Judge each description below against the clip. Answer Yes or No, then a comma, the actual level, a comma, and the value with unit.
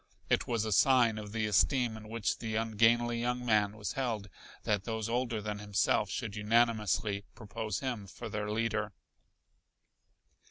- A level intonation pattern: Yes, narrow, 2.0 semitones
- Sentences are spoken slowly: No, average, 155 wpm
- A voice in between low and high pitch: No, low, 110 Hz